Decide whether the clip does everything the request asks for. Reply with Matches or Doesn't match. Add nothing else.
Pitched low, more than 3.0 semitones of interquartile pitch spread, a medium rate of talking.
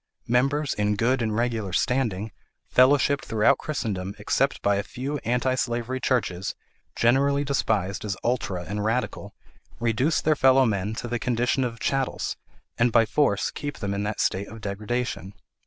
Matches